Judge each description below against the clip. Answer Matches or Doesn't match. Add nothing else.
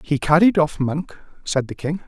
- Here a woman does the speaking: Doesn't match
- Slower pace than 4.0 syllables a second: Doesn't match